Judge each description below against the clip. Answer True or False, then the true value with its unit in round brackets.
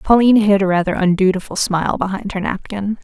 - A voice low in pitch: False (195 Hz)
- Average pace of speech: True (180 wpm)